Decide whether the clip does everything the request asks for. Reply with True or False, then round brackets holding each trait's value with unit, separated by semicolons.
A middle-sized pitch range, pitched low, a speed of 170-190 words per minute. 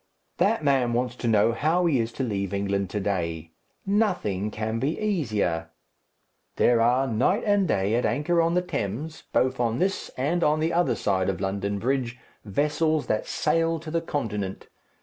False (7.9 semitones; 125 Hz; 175 wpm)